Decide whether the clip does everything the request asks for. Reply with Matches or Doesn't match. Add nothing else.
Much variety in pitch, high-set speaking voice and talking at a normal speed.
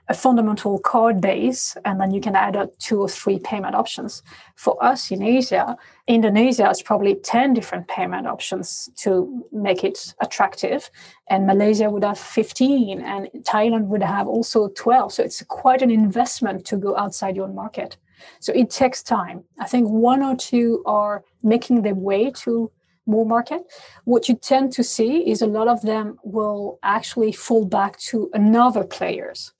Doesn't match